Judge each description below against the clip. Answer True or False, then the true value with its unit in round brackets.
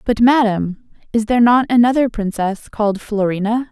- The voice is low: False (225 Hz)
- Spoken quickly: False (145 wpm)